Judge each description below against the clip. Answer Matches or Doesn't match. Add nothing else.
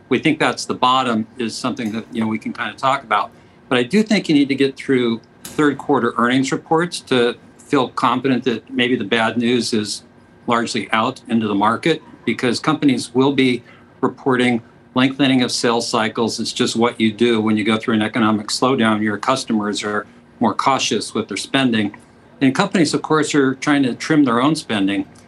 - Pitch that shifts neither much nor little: Matches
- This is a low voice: Matches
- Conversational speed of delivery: Matches